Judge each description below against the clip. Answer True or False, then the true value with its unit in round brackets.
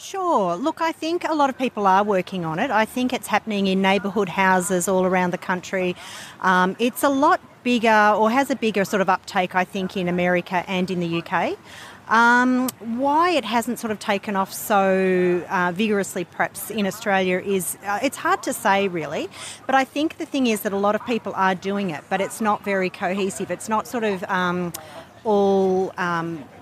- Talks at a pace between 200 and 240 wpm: True (205 wpm)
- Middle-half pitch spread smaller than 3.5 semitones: False (4.2 semitones)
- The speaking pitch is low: False (195 Hz)